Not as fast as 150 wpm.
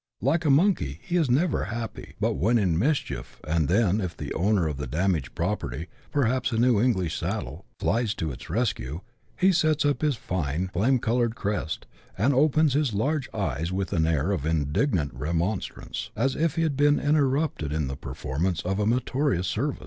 No: average, 185 wpm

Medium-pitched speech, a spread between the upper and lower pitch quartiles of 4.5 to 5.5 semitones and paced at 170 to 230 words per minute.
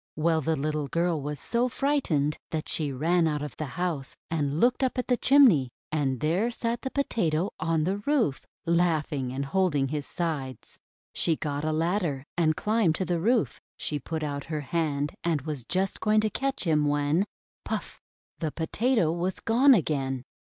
Yes: medium, 160 Hz; average, 4.8 semitones; average, 180 wpm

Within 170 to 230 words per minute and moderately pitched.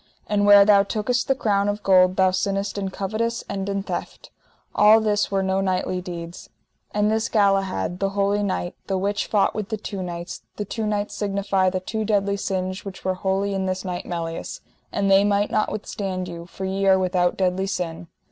No: average, 200 wpm; high, 195 Hz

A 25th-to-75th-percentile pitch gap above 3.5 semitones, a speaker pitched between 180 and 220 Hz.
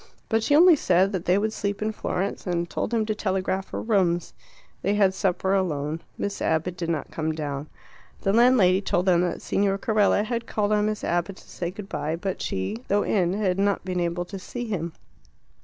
No: average, 3.2 semitones; high, 190 Hz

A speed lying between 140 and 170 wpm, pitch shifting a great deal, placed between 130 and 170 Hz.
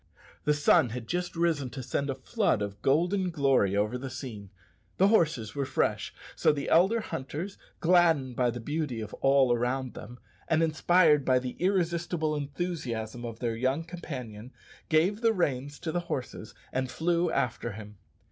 Yes: average, 165 wpm; wide, 5.7 semitones; medium, 140 Hz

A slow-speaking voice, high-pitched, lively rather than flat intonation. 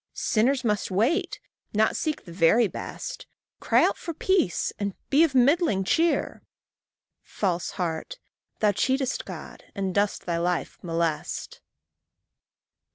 Yes: slow, 125 wpm; high, 210 Hz; wide, 7.2 semitones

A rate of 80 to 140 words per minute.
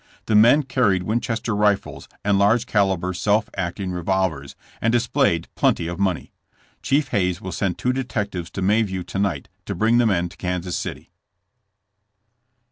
No: average, 155 wpm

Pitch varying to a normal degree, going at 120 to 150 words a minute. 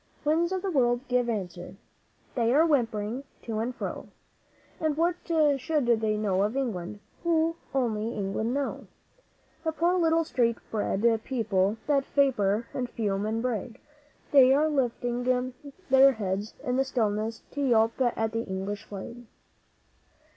Yes: average, 4.3 semitones; average, 145 wpm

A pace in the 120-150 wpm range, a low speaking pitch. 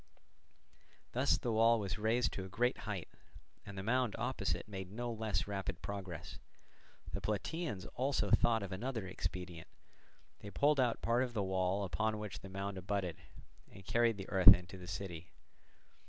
No: average, 165 wpm; low, 100 Hz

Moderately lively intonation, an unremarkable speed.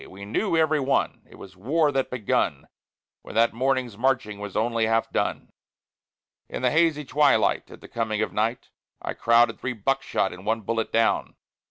Yes: average, 3.8 semitones; average, 175 wpm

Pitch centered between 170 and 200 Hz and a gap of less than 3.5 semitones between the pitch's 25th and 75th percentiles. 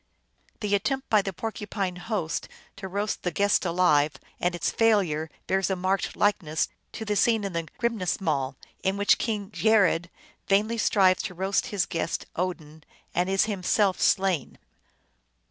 Yes: high, 190 Hz; average, 2.8 semitones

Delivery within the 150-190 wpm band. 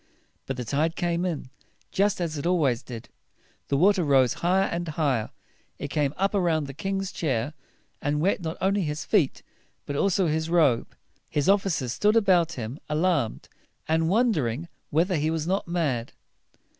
Yes: average, 170 wpm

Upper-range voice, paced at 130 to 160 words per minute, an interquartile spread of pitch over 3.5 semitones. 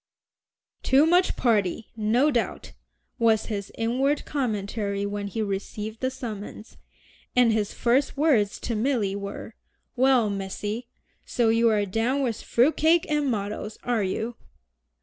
Yes: high, 225 Hz; slow, 135 wpm; average, 3.9 semitones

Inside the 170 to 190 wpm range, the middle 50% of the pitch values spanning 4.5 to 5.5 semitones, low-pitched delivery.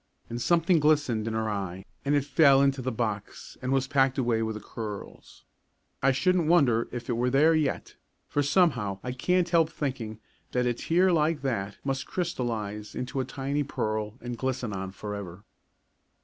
Yes: average, 175 wpm; average, 4.8 semitones; low, 130 Hz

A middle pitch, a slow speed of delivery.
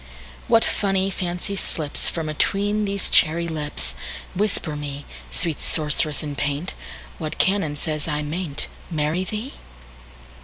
Yes: medium, 160 Hz; slow, 105 wpm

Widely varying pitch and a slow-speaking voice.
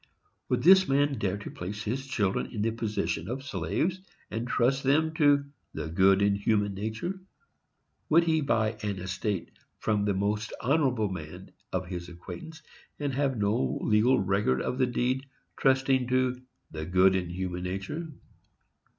No: wide, 5.9 semitones; average, 160 wpm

